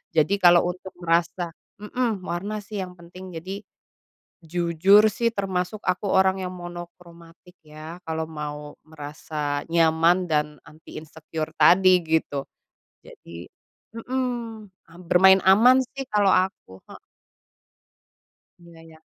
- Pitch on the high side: No, medium, 175 Hz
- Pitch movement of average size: Yes, average, 3.2 semitones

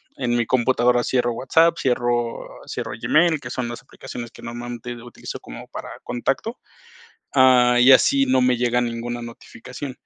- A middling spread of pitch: No, narrow, 1.4 semitones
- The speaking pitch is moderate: No, low, 125 Hz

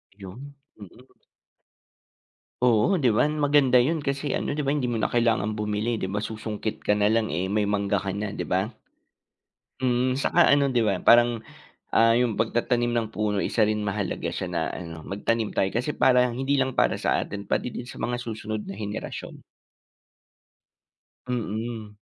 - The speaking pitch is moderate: No, low, 115 Hz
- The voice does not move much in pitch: No, average, 3.2 semitones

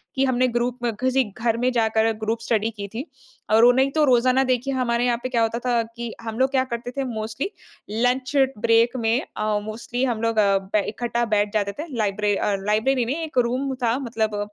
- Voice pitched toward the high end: Yes, high, 235 Hz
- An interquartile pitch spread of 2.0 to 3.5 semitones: Yes, narrow, 2.5 semitones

